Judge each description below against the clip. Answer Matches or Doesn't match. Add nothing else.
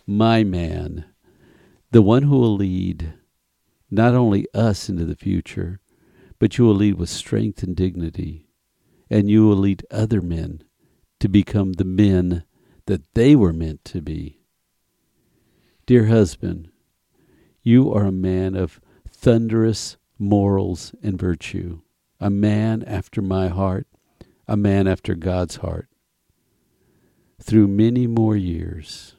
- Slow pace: Matches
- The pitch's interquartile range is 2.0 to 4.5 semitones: Matches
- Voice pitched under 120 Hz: Matches